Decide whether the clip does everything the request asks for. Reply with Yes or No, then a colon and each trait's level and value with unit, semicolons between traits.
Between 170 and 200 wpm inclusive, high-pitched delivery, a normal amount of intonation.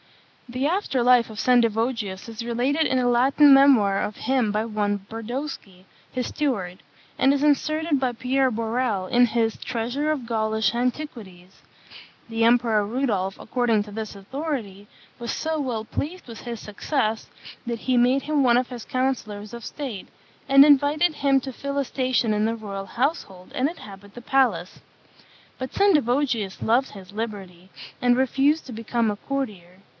No: average, 160 wpm; high, 240 Hz; average, 4.0 semitones